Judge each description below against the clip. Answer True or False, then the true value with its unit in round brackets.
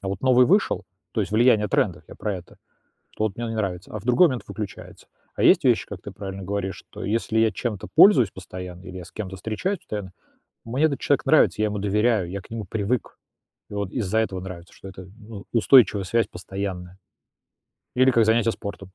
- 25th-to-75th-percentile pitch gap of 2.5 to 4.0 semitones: True (3.4 semitones)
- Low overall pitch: True (105 Hz)